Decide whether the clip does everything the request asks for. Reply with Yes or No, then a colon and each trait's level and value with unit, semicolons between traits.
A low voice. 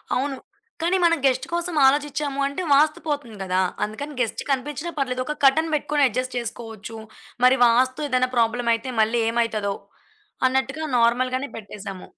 No: very high, 255 Hz